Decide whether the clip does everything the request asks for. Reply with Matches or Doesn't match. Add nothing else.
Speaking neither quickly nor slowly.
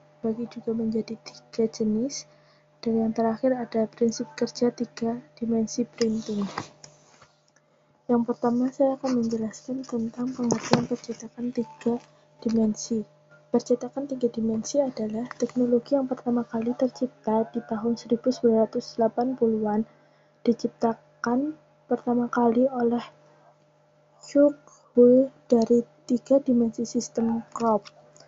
Matches